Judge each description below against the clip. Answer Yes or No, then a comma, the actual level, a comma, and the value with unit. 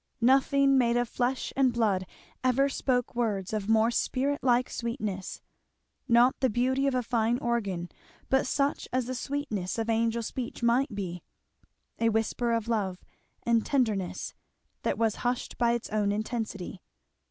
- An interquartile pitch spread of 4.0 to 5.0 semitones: No, average, 2.9 semitones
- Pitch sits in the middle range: No, high, 235 Hz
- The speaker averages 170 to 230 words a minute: No, average, 155 wpm